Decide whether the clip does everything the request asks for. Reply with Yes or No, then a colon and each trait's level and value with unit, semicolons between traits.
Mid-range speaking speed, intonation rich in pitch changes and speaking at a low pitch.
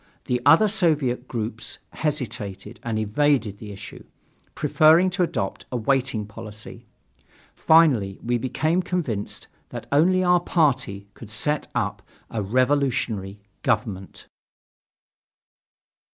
No: slow, 110 wpm; wide, 6.3 semitones; low, 125 Hz